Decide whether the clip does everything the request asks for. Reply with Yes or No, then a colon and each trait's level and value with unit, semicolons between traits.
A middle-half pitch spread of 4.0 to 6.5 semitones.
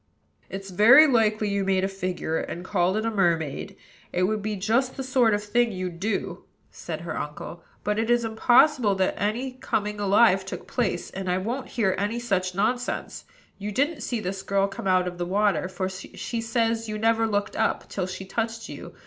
No: average, 3.4 semitones